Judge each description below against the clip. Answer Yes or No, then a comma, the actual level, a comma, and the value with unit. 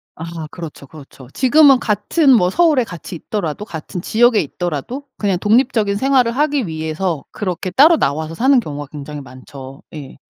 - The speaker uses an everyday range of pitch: No, wide, 8.2 semitones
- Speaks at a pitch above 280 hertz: No, medium, 185 Hz